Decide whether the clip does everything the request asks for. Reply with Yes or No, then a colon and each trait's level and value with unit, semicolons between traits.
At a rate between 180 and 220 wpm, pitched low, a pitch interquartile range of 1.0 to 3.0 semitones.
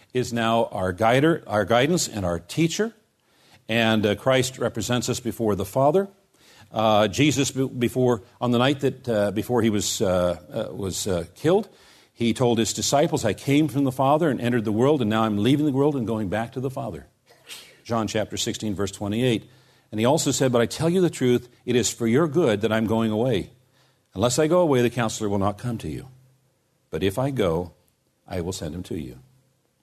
No: fast, 205 wpm; low, 120 Hz; average, 3.6 semitones